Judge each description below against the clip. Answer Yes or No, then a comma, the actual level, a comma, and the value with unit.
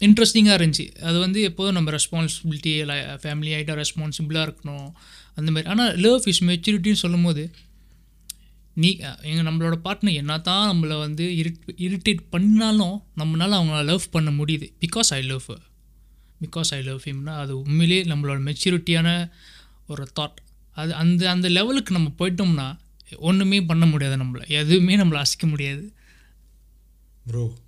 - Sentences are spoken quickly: Yes, fast, 135 wpm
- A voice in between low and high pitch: Yes, medium, 165 Hz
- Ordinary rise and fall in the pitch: Yes, average, 3.5 semitones